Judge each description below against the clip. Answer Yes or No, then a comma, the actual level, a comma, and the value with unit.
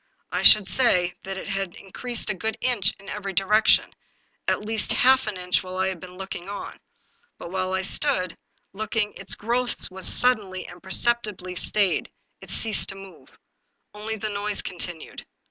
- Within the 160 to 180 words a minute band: Yes, average, 170 wpm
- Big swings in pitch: No, average, 2.8 semitones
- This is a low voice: No, high, 195 Hz